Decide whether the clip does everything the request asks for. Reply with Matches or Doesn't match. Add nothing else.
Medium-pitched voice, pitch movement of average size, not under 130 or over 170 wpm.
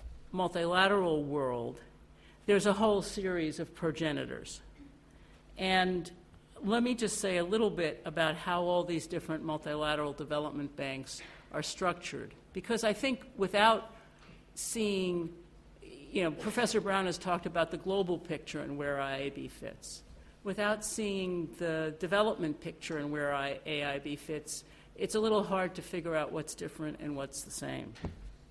Matches